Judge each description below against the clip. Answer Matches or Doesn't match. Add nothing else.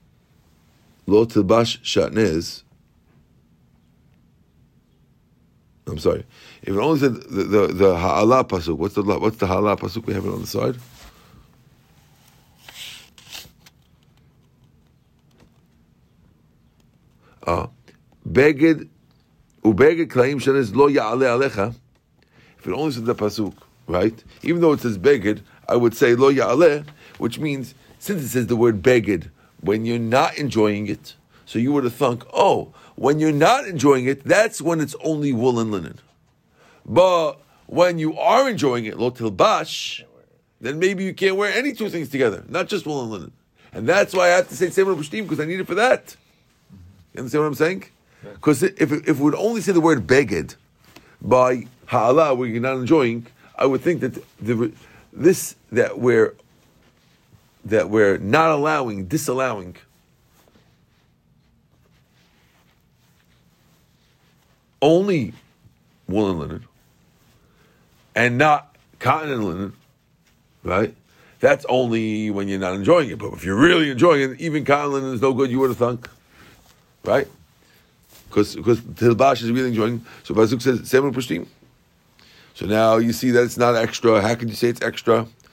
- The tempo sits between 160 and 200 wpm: Doesn't match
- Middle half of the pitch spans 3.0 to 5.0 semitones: Doesn't match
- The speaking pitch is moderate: Doesn't match